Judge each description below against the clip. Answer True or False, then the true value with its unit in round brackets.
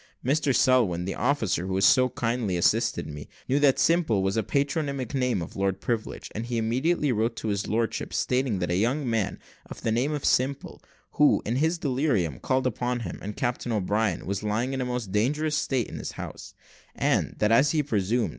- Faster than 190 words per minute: True (200 wpm)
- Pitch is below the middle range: True (120 Hz)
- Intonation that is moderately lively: True (4.4 semitones)